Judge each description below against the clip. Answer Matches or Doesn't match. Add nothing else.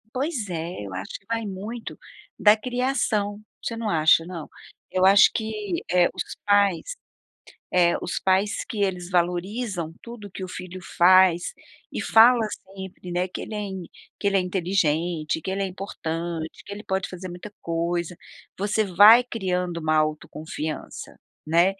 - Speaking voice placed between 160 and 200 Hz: Matches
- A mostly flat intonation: Doesn't match